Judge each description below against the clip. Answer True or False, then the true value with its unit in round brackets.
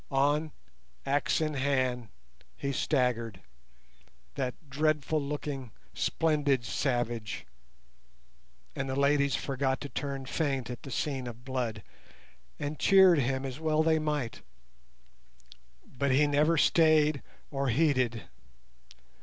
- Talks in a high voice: False (140 Hz)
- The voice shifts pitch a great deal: False (2.7 semitones)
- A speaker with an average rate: False (110 wpm)